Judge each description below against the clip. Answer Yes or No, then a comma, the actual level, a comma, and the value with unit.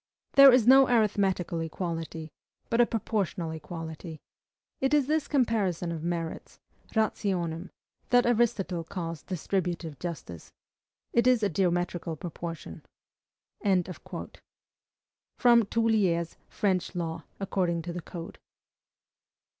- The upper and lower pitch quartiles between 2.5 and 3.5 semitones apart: No, average, 4.9 semitones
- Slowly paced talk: Yes, slow, 100 wpm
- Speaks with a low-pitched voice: No, medium, 180 Hz